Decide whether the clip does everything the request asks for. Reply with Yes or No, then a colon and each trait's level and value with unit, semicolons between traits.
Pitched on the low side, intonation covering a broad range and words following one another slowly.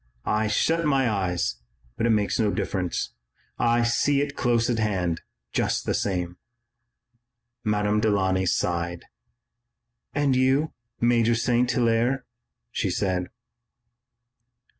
No: low, 115 Hz; average, 4.6 semitones; slow, 115 wpm